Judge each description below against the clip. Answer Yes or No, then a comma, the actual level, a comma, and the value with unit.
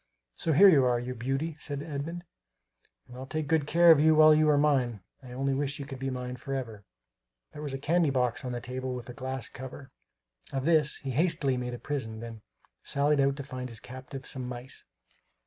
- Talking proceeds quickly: Yes, fast, 215 wpm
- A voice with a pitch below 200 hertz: Yes, low, 135 Hz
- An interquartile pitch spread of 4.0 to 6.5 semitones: No, average, 2.9 semitones